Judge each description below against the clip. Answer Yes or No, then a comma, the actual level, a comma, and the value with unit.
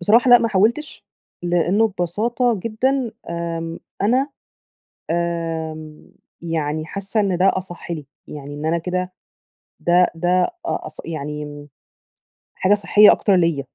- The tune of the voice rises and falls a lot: No, average, 4.3 semitones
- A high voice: No, medium, 175 Hz